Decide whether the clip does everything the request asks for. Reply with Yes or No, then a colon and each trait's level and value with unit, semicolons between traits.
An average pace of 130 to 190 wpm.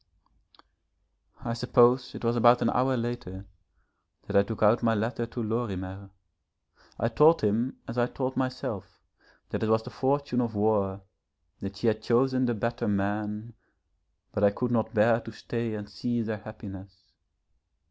Yes: average, 160 wpm